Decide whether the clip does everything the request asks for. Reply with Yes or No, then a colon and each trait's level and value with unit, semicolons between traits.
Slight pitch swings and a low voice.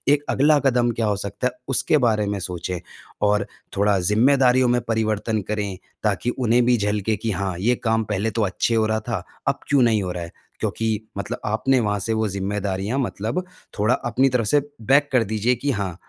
No: average, 3.2 semitones; low, 110 Hz